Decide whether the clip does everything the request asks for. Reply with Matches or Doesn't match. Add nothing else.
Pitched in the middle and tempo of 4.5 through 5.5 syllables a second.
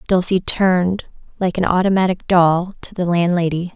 Matches